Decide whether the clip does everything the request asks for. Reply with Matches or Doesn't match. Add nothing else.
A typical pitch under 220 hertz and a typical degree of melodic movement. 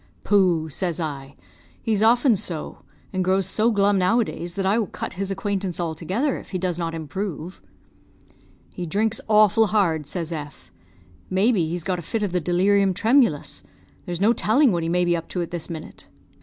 Matches